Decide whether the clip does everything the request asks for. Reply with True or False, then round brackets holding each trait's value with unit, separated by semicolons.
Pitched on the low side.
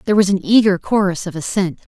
False (190 Hz)